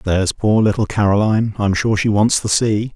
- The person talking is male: Yes, male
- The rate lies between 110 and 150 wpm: No, fast, 205 wpm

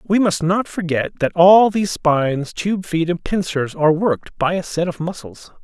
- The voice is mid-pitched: Yes, medium, 170 Hz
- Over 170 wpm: Yes, average, 200 wpm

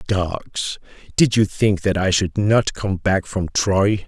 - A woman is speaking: No, male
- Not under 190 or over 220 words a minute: No, average, 175 wpm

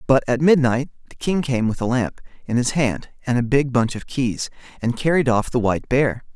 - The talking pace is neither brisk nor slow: No, fast, 225 wpm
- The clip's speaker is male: Yes, male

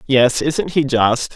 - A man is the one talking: Yes, male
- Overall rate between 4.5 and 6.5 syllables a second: No, 3.3 syllables/s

